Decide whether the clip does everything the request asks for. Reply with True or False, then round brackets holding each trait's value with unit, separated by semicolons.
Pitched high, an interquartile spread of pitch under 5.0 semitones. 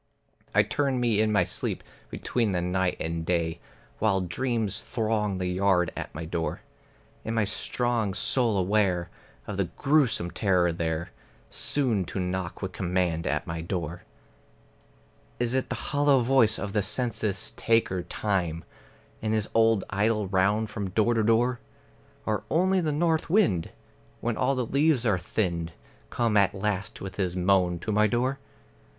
False (105 Hz; 4.5 semitones)